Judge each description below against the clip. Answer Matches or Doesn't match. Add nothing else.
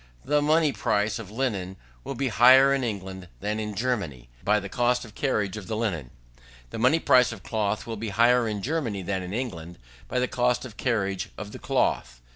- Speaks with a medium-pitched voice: Doesn't match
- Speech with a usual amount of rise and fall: Matches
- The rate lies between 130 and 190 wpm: Doesn't match